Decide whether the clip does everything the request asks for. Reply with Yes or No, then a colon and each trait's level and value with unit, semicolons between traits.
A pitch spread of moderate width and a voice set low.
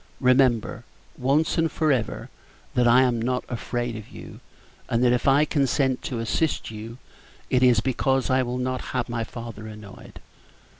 No: narrow, 2.2 semitones; low, 125 Hz